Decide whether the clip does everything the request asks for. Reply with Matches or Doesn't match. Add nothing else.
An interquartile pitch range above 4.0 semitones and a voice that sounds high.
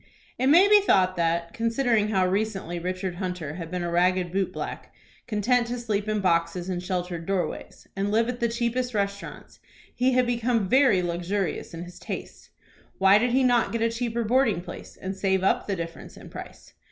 Matches